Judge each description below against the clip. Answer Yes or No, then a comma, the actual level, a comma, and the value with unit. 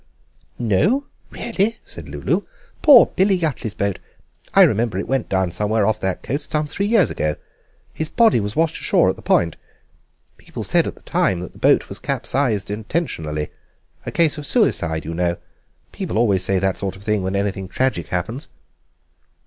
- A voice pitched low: Yes, low, 105 Hz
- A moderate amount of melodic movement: No, wide, 8.4 semitones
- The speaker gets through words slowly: No, average, 175 wpm